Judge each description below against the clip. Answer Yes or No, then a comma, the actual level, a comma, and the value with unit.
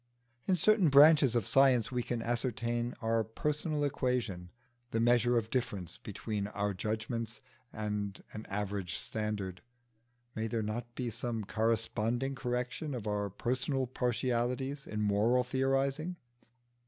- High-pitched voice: No, low, 120 Hz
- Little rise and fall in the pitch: No, average, 3.5 semitones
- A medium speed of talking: No, slow, 130 wpm